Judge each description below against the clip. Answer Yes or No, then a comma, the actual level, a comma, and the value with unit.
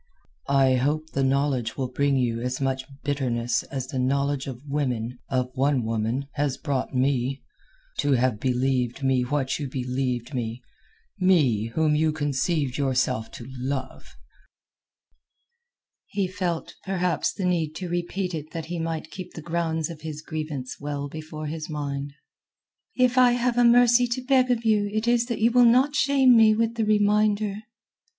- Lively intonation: Yes, wide, 6.3 semitones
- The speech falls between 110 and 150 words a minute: No, average, 160 wpm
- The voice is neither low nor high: Yes, medium, 145 Hz